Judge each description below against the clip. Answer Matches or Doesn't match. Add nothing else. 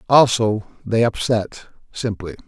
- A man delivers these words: Matches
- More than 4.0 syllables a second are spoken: Doesn't match